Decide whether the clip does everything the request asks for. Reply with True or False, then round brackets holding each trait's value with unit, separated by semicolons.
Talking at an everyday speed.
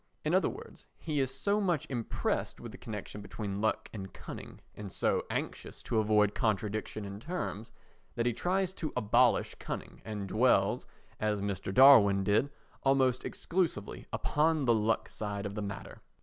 True (165 wpm)